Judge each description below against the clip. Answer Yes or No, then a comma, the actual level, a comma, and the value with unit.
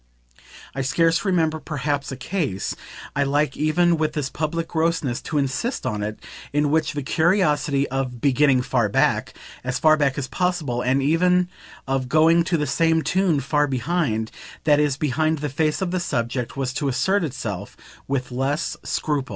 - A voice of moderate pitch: Yes, medium, 145 Hz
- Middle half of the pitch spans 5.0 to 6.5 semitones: No, average, 3.5 semitones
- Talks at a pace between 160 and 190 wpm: Yes, average, 170 wpm